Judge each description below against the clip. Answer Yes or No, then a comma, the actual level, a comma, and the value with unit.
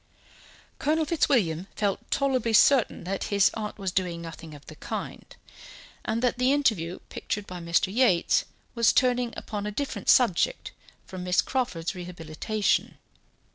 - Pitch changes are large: Yes, wide, 5.9 semitones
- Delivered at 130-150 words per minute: Yes, average, 140 wpm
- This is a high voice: Yes, high, 205 Hz